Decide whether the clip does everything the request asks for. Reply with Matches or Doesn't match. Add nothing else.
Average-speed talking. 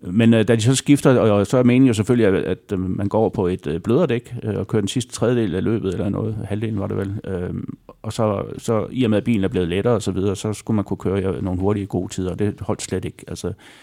Doesn't match